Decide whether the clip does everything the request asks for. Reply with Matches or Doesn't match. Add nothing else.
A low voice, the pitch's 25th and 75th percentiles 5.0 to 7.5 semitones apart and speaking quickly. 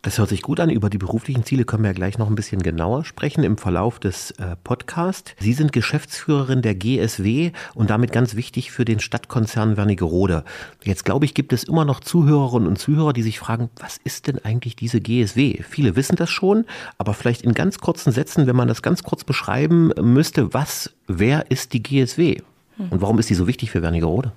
Matches